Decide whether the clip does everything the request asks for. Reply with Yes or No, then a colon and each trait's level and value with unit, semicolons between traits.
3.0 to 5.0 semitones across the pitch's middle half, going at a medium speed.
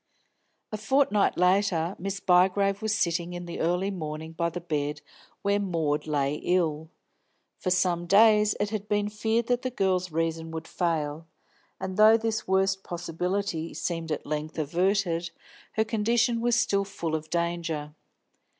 Yes: average, 3.9 semitones; average, 150 wpm